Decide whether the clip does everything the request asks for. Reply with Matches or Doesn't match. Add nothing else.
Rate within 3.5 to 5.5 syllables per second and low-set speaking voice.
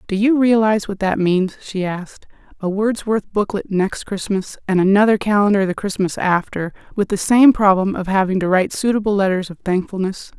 Doesn't match